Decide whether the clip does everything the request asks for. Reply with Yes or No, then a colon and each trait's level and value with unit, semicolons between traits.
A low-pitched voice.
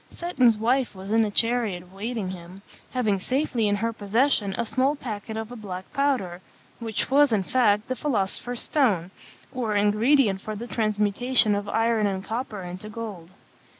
No: high, 220 Hz